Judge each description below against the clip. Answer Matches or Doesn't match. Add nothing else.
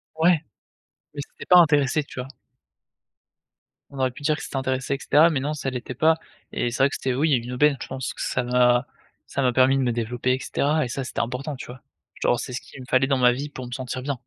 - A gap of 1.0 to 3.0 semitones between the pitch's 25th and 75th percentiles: Matches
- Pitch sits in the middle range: Doesn't match